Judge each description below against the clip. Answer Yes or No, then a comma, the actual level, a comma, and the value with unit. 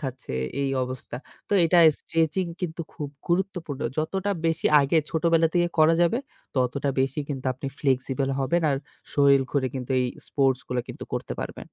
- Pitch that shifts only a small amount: No, average, 3.8 semitones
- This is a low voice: No, medium, 145 Hz